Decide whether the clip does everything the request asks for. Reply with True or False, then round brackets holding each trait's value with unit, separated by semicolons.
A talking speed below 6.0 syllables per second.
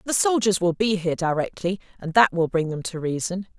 True (5.6 syllables/s)